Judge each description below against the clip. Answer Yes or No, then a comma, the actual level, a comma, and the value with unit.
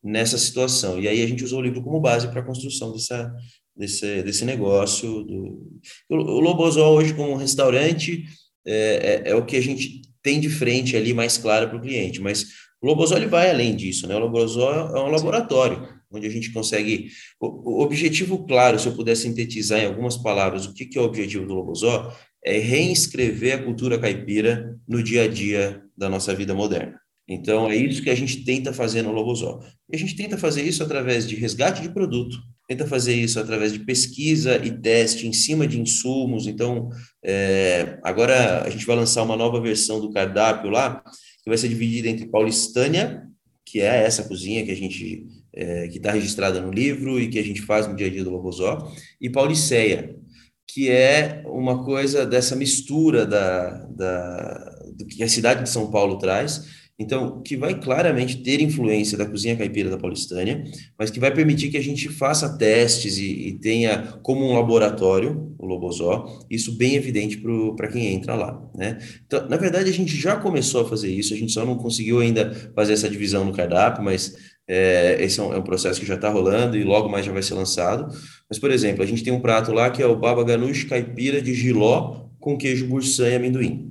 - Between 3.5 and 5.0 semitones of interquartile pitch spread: Yes, average, 3.9 semitones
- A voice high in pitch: No, low, 115 Hz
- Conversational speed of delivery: No, fast, 200 wpm